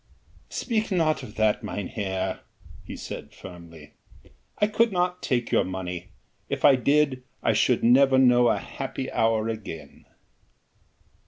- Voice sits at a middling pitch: No, low, 120 Hz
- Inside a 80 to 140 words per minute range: Yes, slow, 135 wpm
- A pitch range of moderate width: No, wide, 5.8 semitones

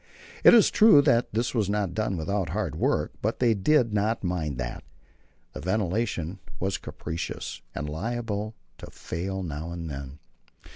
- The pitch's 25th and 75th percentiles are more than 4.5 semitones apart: Yes, average, 5.2 semitones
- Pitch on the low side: Yes, low, 100 Hz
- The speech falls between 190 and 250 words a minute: No, average, 155 wpm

